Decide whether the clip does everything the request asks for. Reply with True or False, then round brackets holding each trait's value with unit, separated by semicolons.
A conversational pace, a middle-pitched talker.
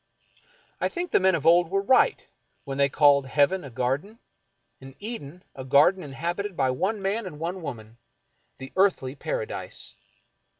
True (160 wpm; 165 Hz)